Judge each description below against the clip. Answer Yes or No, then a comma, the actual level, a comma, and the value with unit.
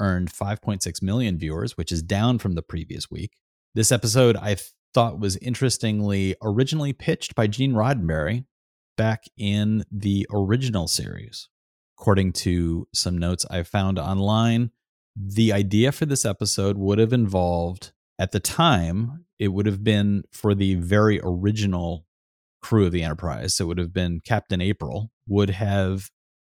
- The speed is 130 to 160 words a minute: Yes, average, 150 wpm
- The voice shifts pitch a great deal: No, average, 3.8 semitones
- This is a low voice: Yes, low, 100 Hz